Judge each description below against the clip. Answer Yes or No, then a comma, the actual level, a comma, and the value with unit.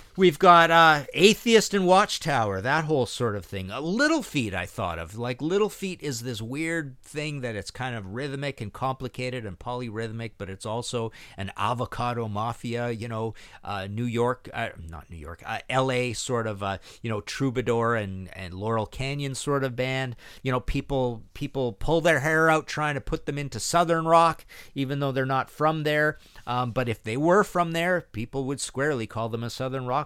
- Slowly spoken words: No, average, 200 wpm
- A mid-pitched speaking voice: No, low, 125 Hz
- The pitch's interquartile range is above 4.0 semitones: Yes, average, 5.0 semitones